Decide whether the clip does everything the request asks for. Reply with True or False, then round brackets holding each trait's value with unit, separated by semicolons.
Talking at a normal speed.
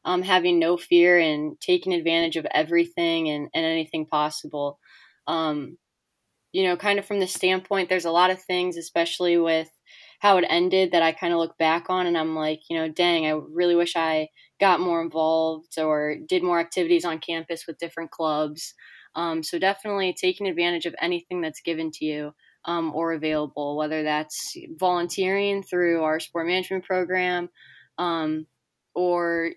True (170 wpm)